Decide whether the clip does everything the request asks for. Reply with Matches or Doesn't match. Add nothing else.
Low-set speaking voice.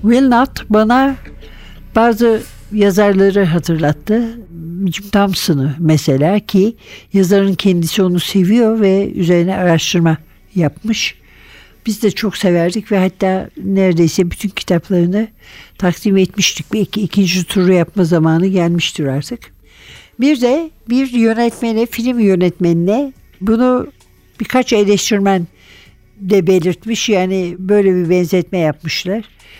Doesn't match